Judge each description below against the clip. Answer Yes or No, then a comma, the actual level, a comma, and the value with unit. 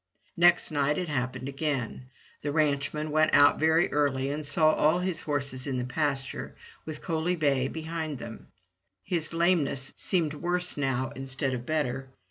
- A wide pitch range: No, average, 3.0 semitones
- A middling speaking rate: Yes, average, 155 wpm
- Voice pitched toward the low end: No, medium, 145 Hz